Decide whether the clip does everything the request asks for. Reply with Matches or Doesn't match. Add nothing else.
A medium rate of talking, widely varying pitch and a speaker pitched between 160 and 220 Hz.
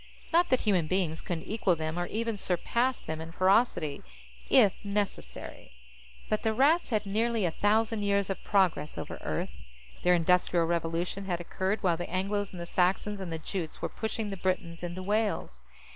Doesn't match